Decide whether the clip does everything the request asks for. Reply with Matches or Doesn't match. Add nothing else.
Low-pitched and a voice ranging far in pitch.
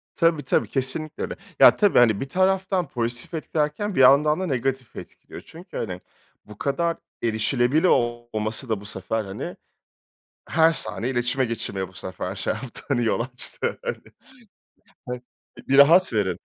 Matches